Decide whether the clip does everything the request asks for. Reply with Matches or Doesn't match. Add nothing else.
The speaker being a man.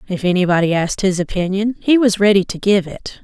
Doesn't match